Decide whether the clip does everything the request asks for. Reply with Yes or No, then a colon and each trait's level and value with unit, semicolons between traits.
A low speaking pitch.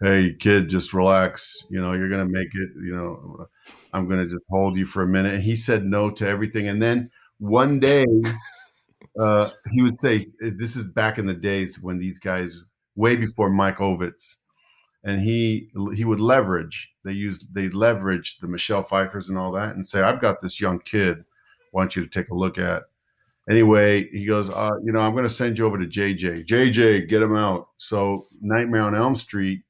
Yes: low, 100 Hz